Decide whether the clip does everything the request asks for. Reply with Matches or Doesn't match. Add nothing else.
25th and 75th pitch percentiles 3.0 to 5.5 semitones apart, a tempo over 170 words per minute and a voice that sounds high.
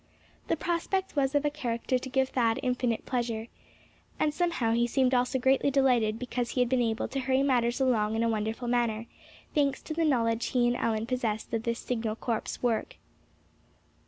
Doesn't match